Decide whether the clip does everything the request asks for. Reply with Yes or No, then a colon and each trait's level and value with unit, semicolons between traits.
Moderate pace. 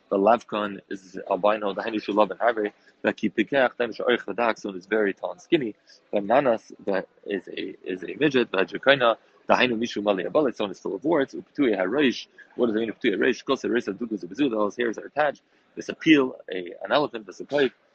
No: fast, 230 wpm